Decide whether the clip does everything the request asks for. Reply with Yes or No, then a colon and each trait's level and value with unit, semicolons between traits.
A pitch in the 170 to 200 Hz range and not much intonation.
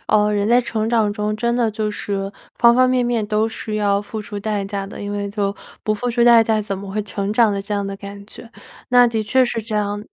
No: high, 210 Hz; narrow, 2.0 semitones